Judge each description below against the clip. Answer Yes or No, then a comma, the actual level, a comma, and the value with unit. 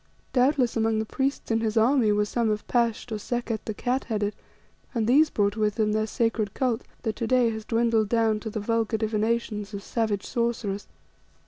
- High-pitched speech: Yes, high, 225 Hz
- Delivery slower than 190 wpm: No, average, 195 wpm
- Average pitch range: No, narrow, 1.9 semitones